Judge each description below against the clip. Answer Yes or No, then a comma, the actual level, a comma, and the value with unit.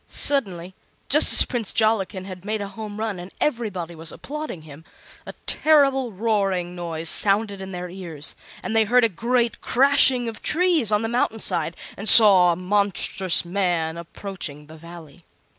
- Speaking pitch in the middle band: No, high, 200 Hz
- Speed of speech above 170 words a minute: No, average, 165 wpm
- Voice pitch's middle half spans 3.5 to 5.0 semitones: Yes, average, 4.5 semitones